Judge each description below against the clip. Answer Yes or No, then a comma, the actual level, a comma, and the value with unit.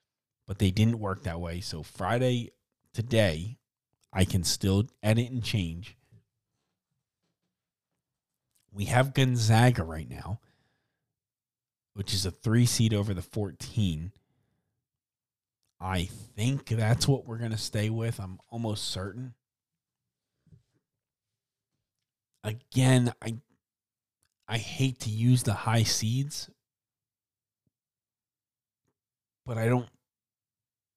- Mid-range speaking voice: No, low, 115 Hz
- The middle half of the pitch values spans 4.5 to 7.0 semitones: No, average, 3.4 semitones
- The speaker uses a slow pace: Yes, slow, 100 wpm